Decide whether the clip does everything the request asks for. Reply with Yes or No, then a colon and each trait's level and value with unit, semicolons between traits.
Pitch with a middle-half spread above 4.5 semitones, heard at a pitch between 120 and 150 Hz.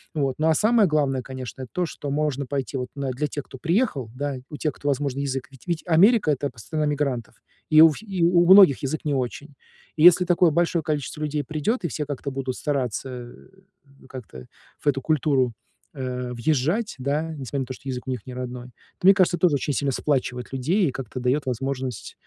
No: average, 3.4 semitones; medium, 140 Hz